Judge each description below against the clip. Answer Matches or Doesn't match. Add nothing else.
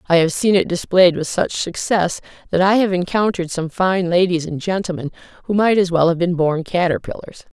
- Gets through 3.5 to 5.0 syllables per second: Doesn't match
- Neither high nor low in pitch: Matches